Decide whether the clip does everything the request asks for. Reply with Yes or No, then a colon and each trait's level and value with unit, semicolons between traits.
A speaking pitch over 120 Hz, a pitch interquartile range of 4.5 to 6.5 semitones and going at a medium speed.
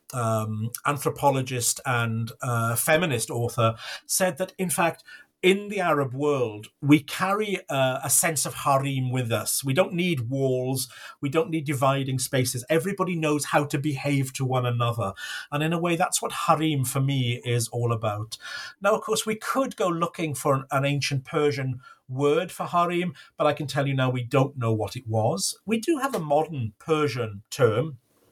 Yes: medium, 140 Hz; average, 5.1 semitones; average, 180 wpm